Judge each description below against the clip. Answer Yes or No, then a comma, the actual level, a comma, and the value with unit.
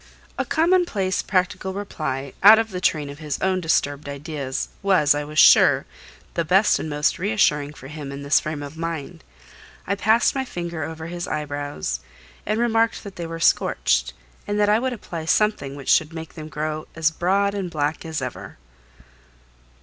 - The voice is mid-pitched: Yes, medium, 160 Hz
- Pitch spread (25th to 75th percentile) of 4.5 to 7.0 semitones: Yes, average, 5.2 semitones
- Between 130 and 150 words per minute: No, average, 180 wpm